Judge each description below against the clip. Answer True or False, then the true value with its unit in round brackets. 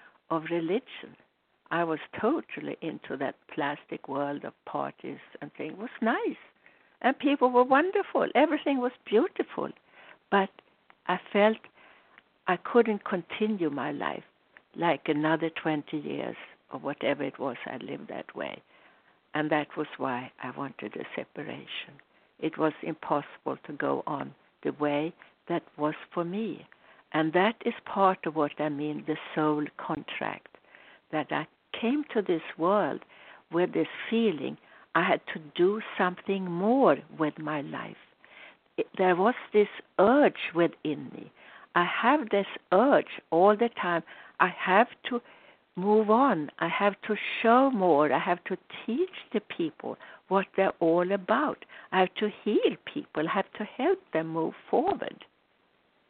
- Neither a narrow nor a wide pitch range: False (6.4 semitones)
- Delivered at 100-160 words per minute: True (145 wpm)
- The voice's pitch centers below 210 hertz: True (190 Hz)